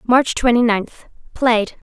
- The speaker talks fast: No, slow, 95 wpm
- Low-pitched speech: No, high, 235 Hz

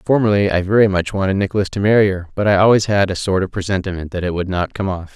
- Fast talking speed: Yes, fast, 270 wpm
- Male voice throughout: Yes, male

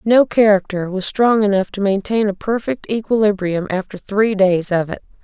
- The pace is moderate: Yes, average, 170 wpm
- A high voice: Yes, high, 205 Hz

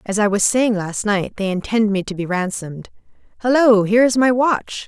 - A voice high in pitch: Yes, high, 210 Hz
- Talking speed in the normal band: No, fast, 210 wpm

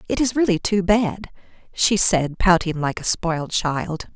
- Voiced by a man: No, female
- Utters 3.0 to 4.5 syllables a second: Yes, 4.2 syllables/s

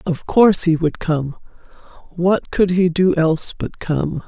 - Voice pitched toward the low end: No, medium, 170 Hz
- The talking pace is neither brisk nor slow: Yes, average, 170 wpm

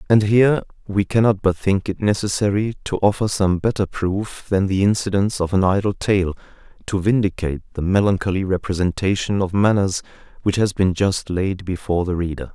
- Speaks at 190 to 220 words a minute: No, average, 165 wpm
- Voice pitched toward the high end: No, very low, 95 Hz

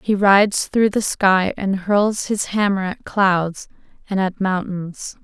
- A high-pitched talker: Yes, high, 195 Hz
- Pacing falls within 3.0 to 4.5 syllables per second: Yes, 3.6 syllables/s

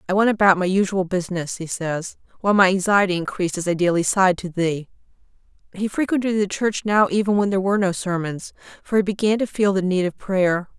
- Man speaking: No, female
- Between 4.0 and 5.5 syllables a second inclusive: No, 6.1 syllables/s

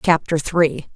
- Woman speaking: Yes, female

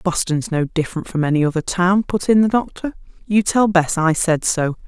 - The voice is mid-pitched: Yes, medium, 180 Hz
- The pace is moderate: No, fast, 210 wpm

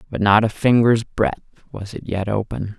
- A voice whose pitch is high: No, low, 105 Hz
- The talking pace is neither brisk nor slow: Yes, average, 195 wpm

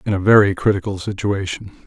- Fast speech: No, average, 160 wpm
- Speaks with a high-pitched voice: No, low, 100 Hz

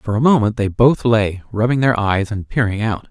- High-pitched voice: No, low, 110 Hz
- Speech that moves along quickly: Yes, fast, 230 wpm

